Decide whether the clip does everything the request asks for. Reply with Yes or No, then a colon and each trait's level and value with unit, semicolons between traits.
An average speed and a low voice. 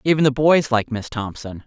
No: fast, 215 wpm; low, 130 Hz